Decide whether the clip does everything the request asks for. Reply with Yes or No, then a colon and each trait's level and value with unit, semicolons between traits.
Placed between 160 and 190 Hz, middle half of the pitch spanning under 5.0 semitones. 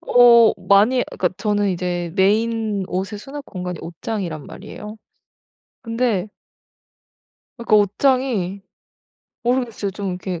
No: high, 205 Hz; average, 3.8 semitones